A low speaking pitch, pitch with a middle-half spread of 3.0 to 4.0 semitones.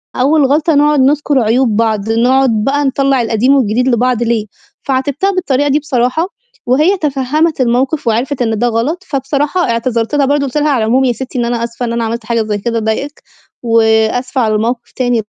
No: very high, 255 Hz; average, 3.6 semitones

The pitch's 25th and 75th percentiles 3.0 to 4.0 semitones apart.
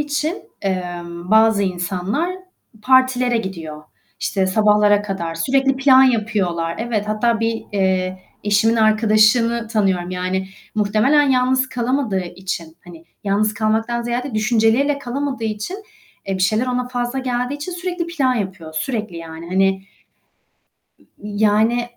No: average, 4.8 semitones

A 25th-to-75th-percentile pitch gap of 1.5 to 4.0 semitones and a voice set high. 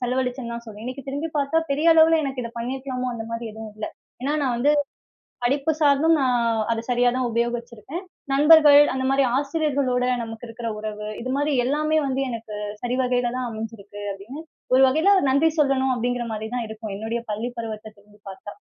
Yes: average, 3.4 semitones; very high, 250 Hz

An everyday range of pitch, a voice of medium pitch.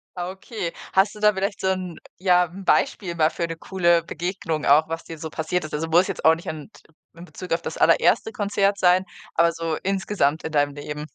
Yes: average, 3.0 semitones; medium, 175 Hz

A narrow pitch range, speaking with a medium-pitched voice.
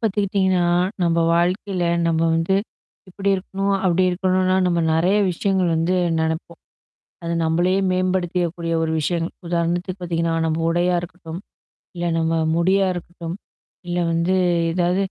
Yes: narrow, 1.8 semitones; medium, 175 Hz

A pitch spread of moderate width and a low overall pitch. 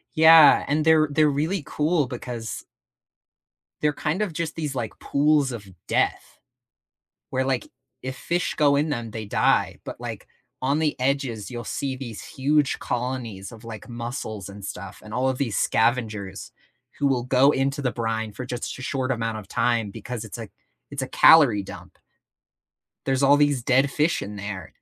Yes: average, 4.2 semitones; low, 130 Hz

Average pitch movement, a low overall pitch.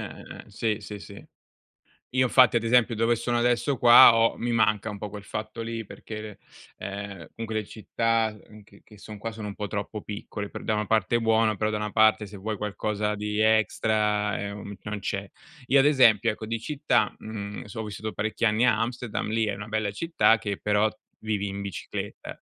No: narrow, 1.6 semitones; low, 110 Hz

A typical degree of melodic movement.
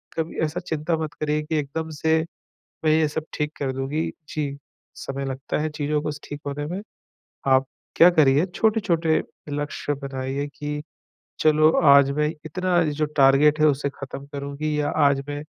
No: narrow, 1.9 semitones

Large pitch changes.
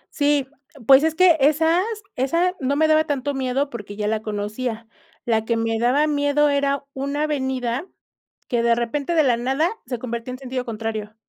No: average, 4.0 semitones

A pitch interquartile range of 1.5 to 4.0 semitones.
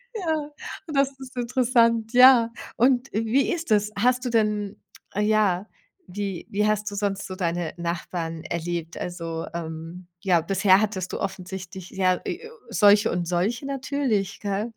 No: average, 4.7 semitones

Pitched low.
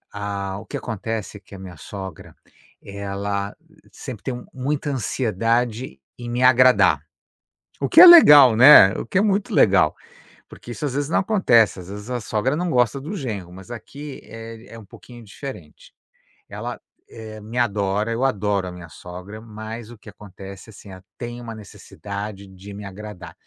Yes: low, 110 Hz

